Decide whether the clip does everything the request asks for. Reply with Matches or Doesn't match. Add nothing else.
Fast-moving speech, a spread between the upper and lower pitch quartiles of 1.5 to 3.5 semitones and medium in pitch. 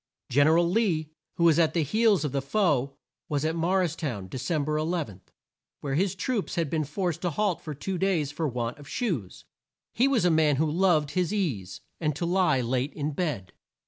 Doesn't match